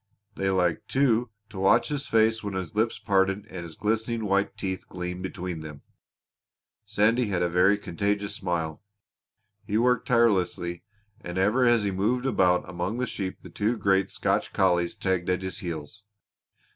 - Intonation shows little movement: No, average, 3.6 semitones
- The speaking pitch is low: Yes, very low, 95 Hz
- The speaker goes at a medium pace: Yes, average, 160 wpm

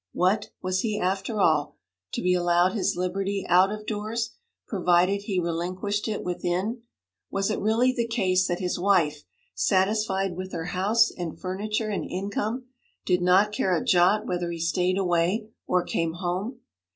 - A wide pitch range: No, average, 2.9 semitones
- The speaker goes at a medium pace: Yes, average, 165 wpm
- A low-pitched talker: No, high, 190 Hz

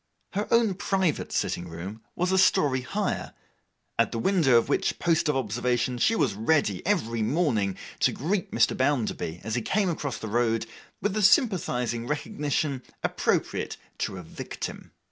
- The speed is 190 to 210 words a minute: No, average, 160 wpm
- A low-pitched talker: Yes, low, 130 Hz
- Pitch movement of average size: No, wide, 7.9 semitones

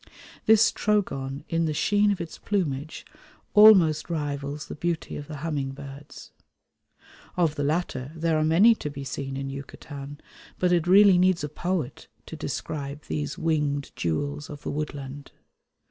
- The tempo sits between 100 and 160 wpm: Yes, average, 155 wpm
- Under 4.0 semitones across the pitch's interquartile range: Yes, average, 3.6 semitones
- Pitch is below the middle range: No, medium, 150 Hz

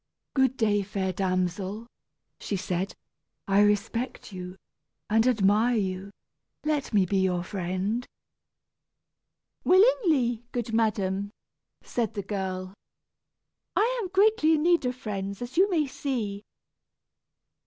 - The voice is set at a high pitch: Yes, high, 210 Hz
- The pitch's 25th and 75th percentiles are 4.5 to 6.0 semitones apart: Yes, average, 5.2 semitones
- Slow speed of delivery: Yes, slow, 115 wpm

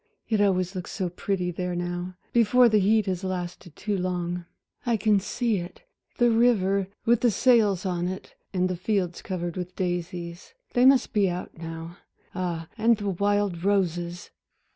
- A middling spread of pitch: Yes, average, 3.0 semitones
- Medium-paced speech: Yes, average, 165 wpm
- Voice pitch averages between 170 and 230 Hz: Yes, medium, 185 Hz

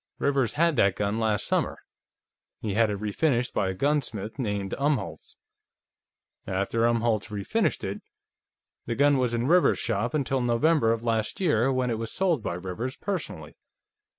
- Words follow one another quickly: No, average, 155 wpm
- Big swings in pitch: No, average, 4.7 semitones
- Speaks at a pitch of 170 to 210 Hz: No, low, 115 Hz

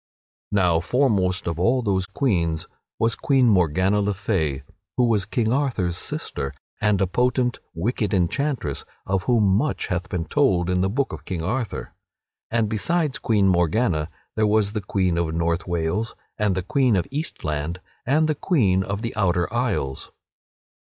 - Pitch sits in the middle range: No, low, 100 Hz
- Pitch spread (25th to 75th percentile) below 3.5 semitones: No, average, 5.3 semitones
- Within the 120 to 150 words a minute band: No, average, 160 wpm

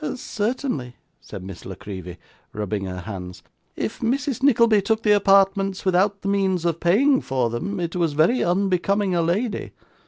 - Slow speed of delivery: No, average, 160 wpm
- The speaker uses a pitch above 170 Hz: Yes, high, 190 Hz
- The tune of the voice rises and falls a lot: Yes, wide, 8.9 semitones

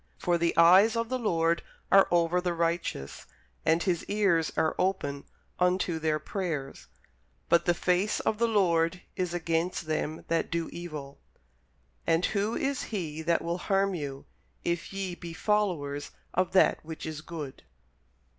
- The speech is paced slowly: No, average, 155 wpm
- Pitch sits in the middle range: Yes, medium, 170 Hz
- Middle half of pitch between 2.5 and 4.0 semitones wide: Yes, average, 2.8 semitones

